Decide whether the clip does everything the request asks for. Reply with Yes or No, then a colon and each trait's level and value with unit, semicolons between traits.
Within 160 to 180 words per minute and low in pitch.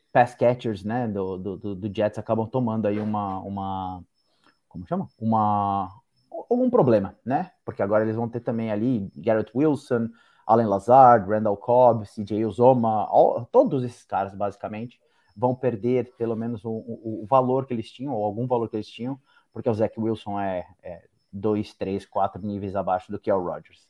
Yes: average, 175 wpm; low, 110 Hz